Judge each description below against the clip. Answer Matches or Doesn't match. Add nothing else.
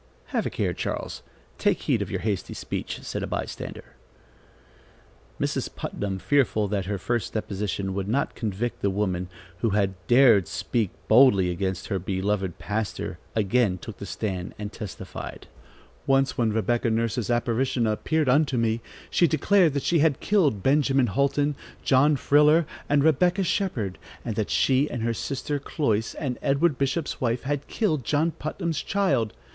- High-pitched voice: Doesn't match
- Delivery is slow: Doesn't match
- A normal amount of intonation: Doesn't match